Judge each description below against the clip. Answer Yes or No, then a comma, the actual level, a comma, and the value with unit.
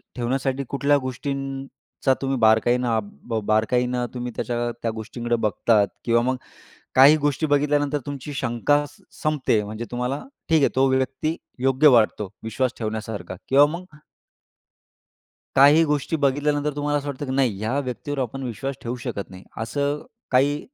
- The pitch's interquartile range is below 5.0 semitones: Yes, average, 3.4 semitones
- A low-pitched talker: Yes, low, 130 Hz